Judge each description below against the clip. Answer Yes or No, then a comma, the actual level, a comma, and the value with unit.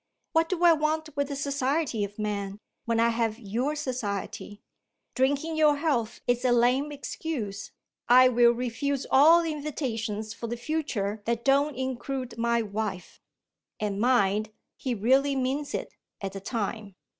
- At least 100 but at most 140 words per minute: No, average, 150 wpm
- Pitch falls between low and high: No, high, 245 Hz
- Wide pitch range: No, average, 4.6 semitones